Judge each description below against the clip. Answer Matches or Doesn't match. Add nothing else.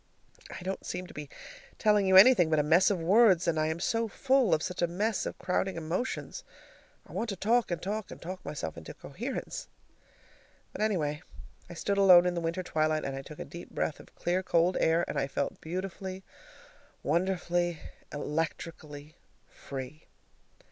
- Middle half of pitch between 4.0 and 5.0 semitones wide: Doesn't match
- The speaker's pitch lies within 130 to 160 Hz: Doesn't match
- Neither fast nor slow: Matches